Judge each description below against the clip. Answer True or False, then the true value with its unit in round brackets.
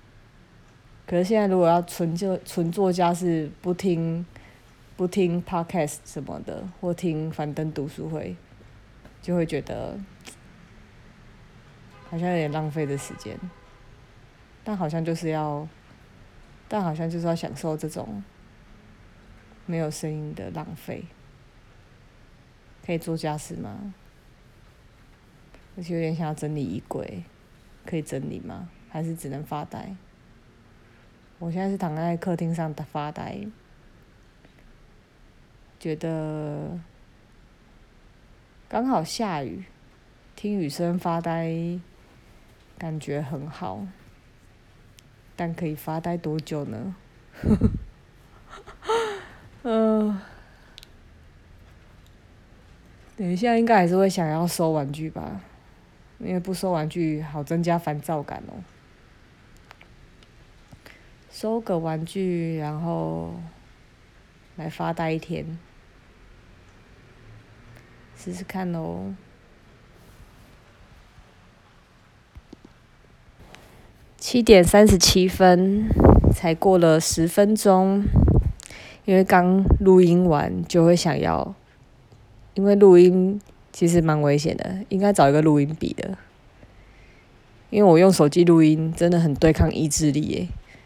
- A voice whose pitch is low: False (160 Hz)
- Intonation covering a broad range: True (6.4 semitones)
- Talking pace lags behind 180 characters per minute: True (155 characters per minute)